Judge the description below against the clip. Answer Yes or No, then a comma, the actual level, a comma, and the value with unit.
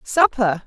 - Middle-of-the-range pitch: No, high, 230 Hz